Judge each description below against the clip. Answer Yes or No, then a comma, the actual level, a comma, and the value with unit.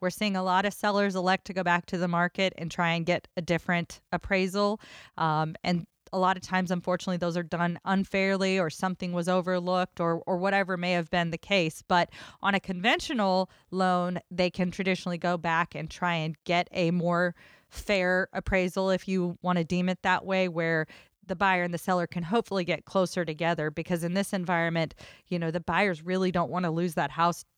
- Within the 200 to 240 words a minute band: Yes, fast, 205 wpm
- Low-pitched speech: No, medium, 180 Hz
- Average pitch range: No, narrow, 1.5 semitones